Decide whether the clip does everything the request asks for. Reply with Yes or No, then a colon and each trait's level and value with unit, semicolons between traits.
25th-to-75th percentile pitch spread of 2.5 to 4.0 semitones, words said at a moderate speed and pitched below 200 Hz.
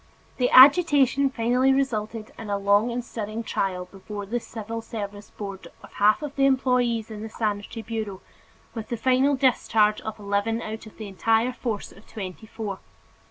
No: average, 3.1 semitones; average, 170 wpm; high, 225 Hz